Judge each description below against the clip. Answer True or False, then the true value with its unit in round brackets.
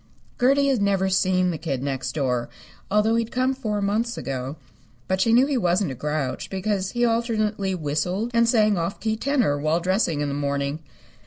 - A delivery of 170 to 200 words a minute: True (190 wpm)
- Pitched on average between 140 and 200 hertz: True (190 Hz)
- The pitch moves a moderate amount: False (7.1 semitones)